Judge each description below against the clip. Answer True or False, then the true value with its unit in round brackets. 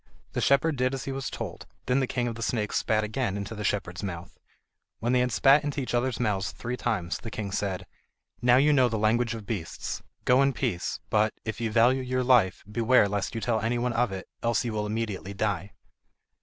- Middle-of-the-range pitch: False (115 Hz)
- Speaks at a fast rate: True (225 wpm)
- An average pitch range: True (3.2 semitones)